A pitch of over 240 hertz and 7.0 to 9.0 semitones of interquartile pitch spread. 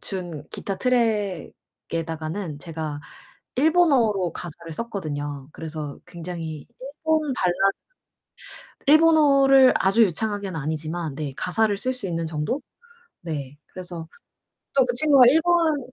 No: medium, 185 Hz; wide, 8.2 semitones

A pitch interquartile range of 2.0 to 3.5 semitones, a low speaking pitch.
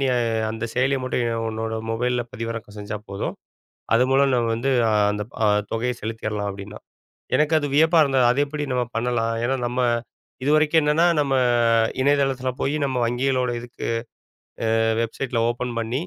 Yes: average, 3.2 semitones; low, 125 Hz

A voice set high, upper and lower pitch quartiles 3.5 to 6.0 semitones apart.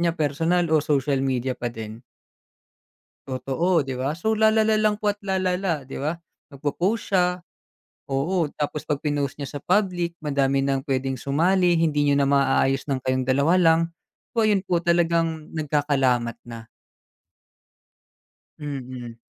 No: medium, 150 Hz; average, 4.7 semitones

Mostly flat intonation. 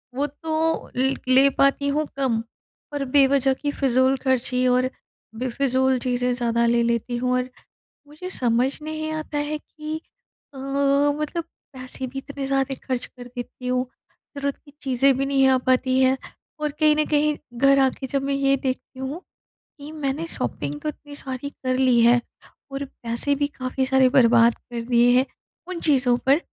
Yes: narrow, 2.2 semitones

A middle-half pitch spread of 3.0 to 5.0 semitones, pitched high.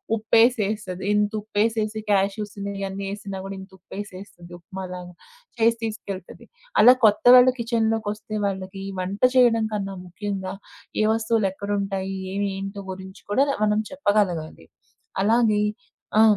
No: narrow, 2.4 semitones; high, 205 Hz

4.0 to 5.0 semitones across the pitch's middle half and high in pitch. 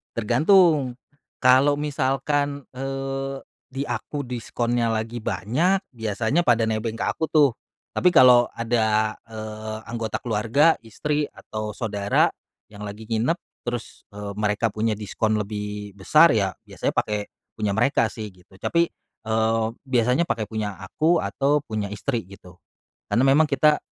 No: average, 4.3 semitones; low, 115 Hz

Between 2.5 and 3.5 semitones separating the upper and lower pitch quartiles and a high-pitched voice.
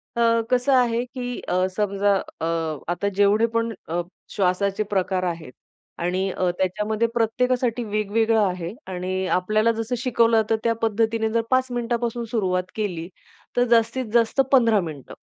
No: average, 3.9 semitones; high, 220 Hz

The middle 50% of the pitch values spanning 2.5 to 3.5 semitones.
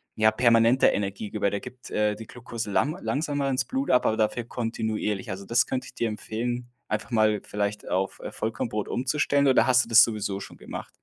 Yes: average, 2.9 semitones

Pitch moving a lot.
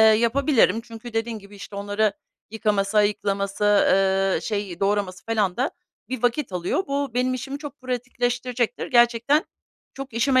No: average, 3.7 semitones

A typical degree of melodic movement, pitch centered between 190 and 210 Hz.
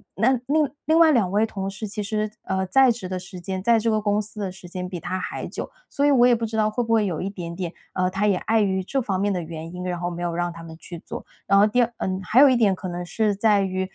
Yes: average, 3.5 semitones; high, 195 Hz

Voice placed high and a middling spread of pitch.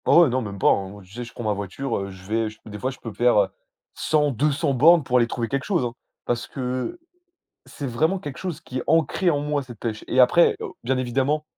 No: low, 125 Hz; average, 4.2 semitones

